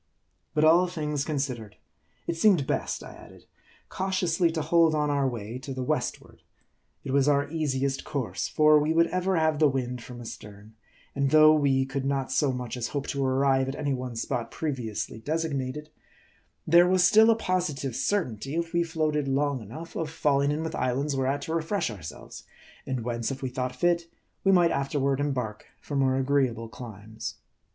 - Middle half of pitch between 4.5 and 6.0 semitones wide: No, average, 3.7 semitones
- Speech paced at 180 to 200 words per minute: Yes, average, 185 wpm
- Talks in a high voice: No, medium, 140 Hz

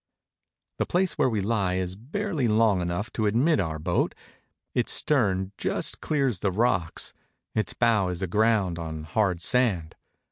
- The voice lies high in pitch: No, low, 105 Hz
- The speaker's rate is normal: Yes, average, 150 wpm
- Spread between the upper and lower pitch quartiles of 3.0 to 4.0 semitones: No, average, 4.8 semitones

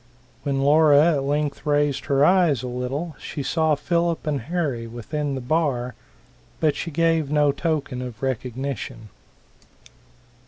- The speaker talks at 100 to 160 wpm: Yes, slow, 135 wpm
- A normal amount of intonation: Yes, average, 3.1 semitones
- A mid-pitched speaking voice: Yes, medium, 145 Hz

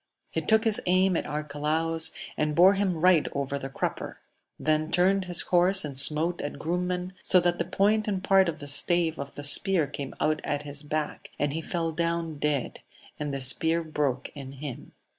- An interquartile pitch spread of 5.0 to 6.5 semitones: No, average, 3.5 semitones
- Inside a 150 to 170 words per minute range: No, average, 195 wpm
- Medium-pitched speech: Yes, medium, 160 Hz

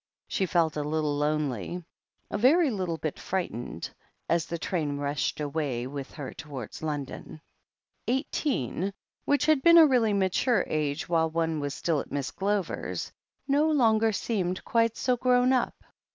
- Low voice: No, medium, 170 Hz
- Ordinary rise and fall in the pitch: No, wide, 7.7 semitones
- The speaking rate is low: No, average, 150 wpm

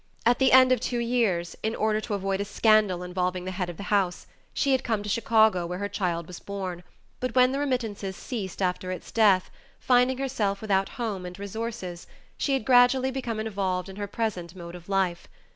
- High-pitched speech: Yes, high, 205 Hz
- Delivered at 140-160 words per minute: No, fast, 205 wpm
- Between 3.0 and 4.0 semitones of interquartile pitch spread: No, average, 4.4 semitones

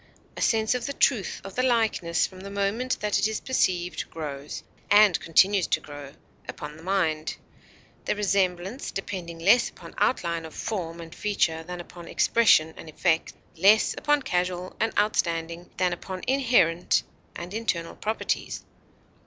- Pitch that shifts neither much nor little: Yes, average, 4.2 semitones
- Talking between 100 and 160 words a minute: Yes, average, 155 wpm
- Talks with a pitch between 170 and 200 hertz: Yes, medium, 185 Hz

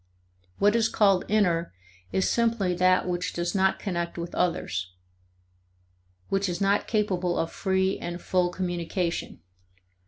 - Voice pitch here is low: No, medium, 185 Hz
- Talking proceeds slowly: Yes, slow, 130 wpm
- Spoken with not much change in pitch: Yes, narrow, 2.2 semitones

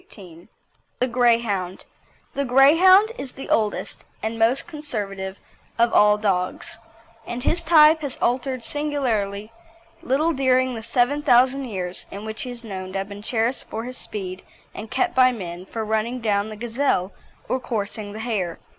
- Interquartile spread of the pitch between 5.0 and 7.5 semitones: No, average, 4.4 semitones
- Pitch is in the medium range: No, high, 230 Hz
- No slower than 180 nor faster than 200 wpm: No, average, 165 wpm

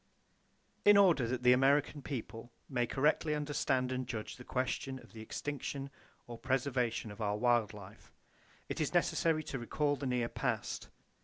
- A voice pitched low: Yes, low, 130 Hz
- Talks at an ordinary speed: Yes, average, 160 wpm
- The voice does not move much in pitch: No, average, 3.3 semitones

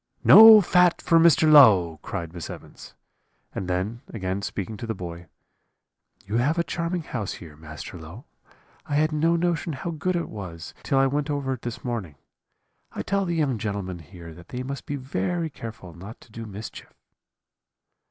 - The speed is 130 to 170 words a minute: No, average, 180 wpm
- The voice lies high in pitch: No, low, 115 Hz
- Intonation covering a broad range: Yes, wide, 9.0 semitones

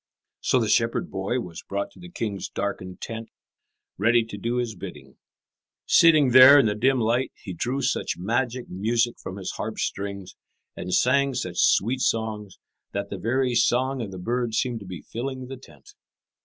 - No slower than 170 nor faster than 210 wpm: Yes, average, 180 wpm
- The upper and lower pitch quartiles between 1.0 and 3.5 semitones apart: No, average, 4.2 semitones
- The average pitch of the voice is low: Yes, low, 115 Hz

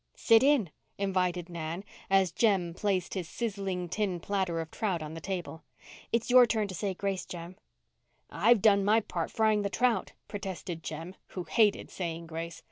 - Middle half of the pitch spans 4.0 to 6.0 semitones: No, average, 3.5 semitones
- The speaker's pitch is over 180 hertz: Yes, high, 190 Hz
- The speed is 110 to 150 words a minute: No, average, 170 wpm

